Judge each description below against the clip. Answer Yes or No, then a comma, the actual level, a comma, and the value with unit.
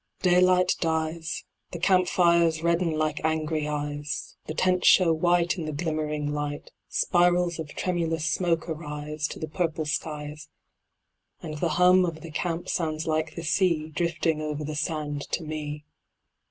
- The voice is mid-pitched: Yes, medium, 160 Hz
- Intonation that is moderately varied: No, narrow, 2.1 semitones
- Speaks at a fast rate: No, average, 155 wpm